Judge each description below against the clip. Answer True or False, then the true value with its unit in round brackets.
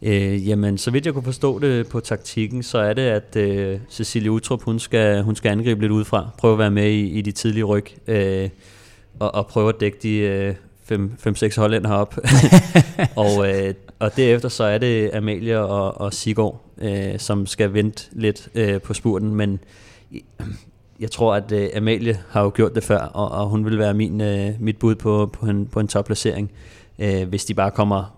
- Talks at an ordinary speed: True (195 wpm)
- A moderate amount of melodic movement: False (1.7 semitones)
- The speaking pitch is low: True (105 Hz)